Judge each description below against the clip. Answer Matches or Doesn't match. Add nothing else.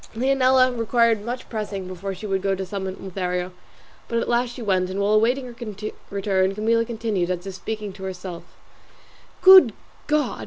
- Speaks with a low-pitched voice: Doesn't match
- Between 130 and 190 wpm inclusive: Matches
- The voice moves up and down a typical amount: Matches